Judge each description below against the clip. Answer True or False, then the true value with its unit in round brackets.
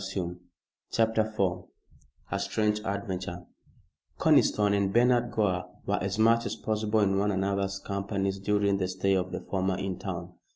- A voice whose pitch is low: True (100 Hz)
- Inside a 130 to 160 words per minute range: True (150 wpm)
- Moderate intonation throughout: False (2.0 semitones)